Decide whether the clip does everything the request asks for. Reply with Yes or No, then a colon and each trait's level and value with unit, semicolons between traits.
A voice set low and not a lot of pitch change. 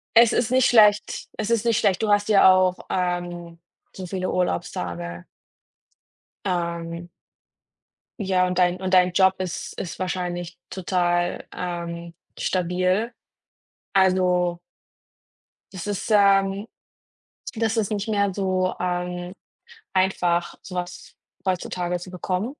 No: medium, 185 Hz; narrow, 1.9 semitones